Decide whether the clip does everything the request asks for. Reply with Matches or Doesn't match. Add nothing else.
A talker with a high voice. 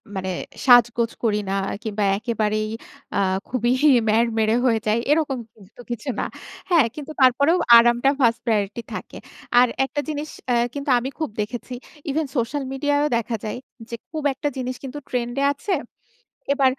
Matches